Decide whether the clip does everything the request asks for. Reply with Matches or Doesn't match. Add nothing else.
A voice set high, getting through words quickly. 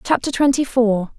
Doesn't match